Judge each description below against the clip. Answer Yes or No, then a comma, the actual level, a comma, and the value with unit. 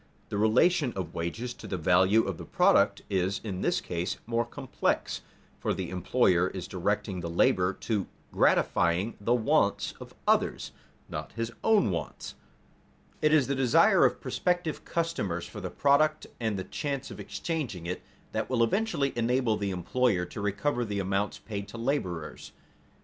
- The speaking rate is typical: Yes, average, 165 wpm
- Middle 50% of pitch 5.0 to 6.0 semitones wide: Yes, wide, 5.5 semitones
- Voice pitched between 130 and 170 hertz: No, low, 105 Hz